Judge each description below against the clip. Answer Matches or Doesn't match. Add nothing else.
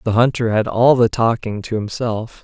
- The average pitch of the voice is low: Matches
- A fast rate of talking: Doesn't match